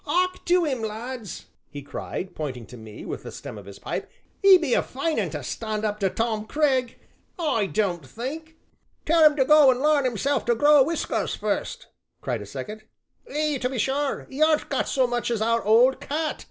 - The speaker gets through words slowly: No, fast, 205 wpm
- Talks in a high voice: Yes, very high, 255 Hz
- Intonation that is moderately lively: No, wide, 5.8 semitones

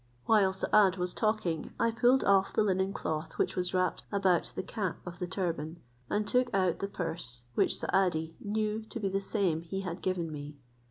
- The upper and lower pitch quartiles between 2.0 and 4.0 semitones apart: Yes, average, 3.2 semitones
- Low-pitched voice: No, high, 190 Hz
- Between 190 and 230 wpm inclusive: Yes, average, 195 wpm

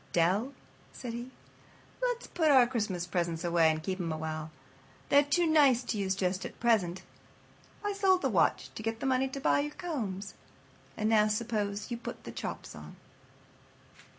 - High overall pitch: Yes, high, 220 Hz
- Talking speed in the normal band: Yes, average, 180 wpm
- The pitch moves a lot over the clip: Yes, wide, 6.7 semitones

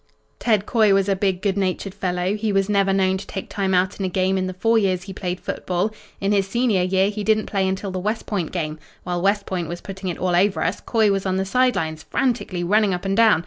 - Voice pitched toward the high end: Yes, high, 195 Hz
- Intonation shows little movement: Yes, narrow, 1.9 semitones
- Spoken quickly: Yes, fast, 260 wpm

